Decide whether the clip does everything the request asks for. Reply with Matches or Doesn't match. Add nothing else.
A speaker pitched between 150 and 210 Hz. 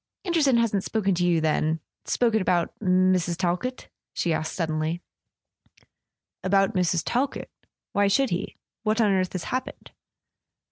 Matches